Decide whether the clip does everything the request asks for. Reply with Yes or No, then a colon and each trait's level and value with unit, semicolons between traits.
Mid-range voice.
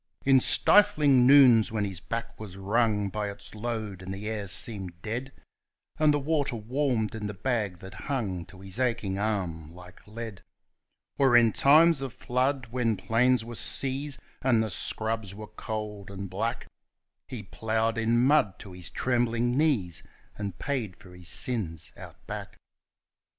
No: low, 110 Hz